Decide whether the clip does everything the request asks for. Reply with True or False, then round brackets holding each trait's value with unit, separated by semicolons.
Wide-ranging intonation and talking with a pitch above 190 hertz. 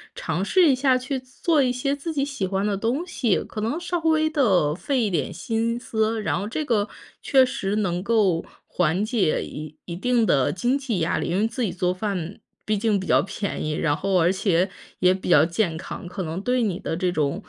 True (5.9 semitones; 210 Hz)